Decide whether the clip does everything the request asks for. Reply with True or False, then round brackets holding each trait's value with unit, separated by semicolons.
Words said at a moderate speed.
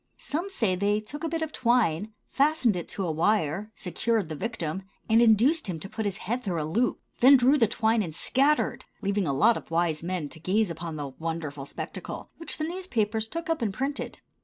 False (210 wpm)